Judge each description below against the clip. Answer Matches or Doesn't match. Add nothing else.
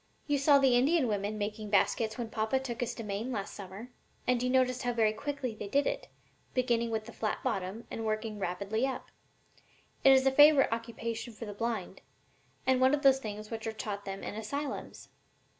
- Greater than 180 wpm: Matches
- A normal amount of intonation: Matches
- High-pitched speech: Matches